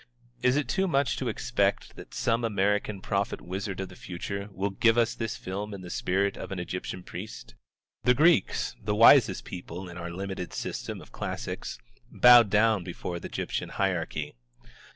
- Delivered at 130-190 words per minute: Yes, average, 175 wpm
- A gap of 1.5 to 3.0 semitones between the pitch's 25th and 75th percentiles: No, average, 3.8 semitones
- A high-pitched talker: No, low, 100 Hz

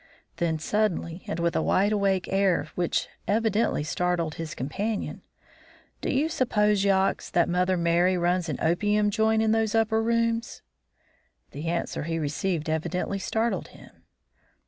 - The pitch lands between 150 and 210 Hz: Yes, high, 190 Hz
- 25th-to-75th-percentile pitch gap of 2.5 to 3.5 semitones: No, average, 4.3 semitones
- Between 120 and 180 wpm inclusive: Yes, average, 145 wpm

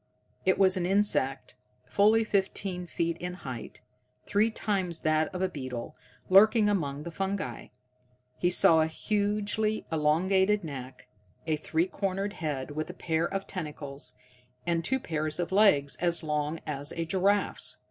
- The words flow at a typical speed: Yes, average, 145 wpm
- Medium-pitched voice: Yes, medium, 175 Hz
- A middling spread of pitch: Yes, average, 4.5 semitones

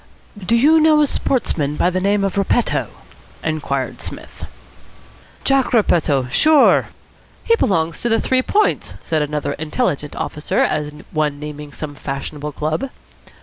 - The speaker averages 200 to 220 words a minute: No, average, 140 wpm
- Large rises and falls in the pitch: Yes, wide, 8.4 semitones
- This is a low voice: No, medium, 160 Hz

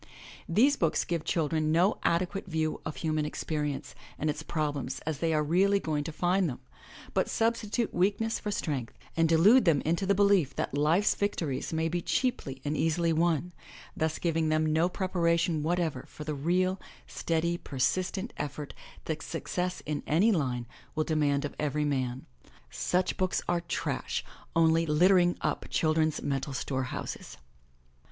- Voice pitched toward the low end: No, medium, 160 Hz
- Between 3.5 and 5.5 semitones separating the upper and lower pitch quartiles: No, average, 3.0 semitones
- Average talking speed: Yes, average, 165 wpm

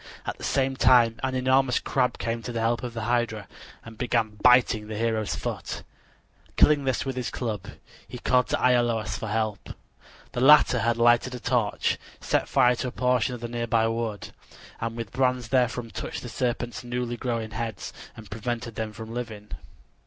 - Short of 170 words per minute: No, average, 180 wpm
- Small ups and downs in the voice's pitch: Yes, narrow, 1.9 semitones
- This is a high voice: No, low, 120 Hz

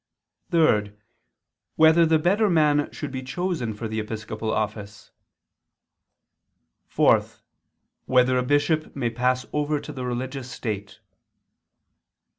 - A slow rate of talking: Yes, slow, 110 wpm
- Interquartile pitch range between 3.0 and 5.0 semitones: No, wide, 5.6 semitones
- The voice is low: Yes, low, 130 Hz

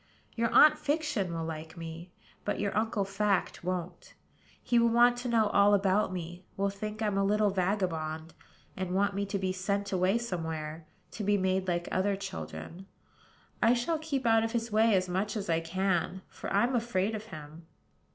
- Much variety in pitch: No, average, 3.4 semitones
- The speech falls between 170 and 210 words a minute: Yes, average, 185 wpm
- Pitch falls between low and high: No, high, 195 Hz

